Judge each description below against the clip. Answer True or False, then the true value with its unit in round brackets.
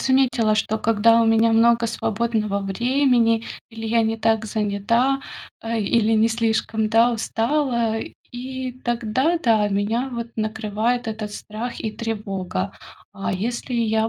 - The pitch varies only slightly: True (1.7 semitones)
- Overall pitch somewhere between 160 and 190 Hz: False (225 Hz)